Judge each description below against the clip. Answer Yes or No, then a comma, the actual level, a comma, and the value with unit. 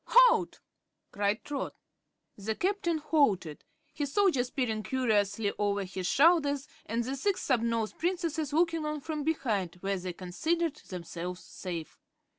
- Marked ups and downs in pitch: Yes, wide, 7.9 semitones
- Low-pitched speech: No, very high, 255 Hz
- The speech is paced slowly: Yes, slow, 130 wpm